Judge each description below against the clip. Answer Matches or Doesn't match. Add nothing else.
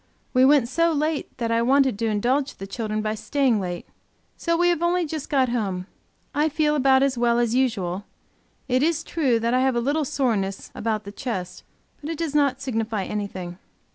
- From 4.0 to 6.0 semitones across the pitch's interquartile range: Matches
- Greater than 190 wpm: Matches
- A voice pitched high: Matches